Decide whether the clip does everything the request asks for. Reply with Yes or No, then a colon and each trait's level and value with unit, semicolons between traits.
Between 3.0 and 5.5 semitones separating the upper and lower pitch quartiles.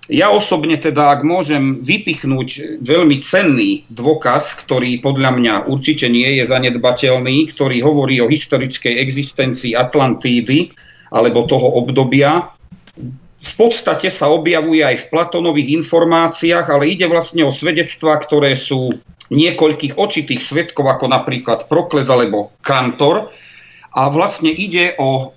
Yes: average, 3.9 semitones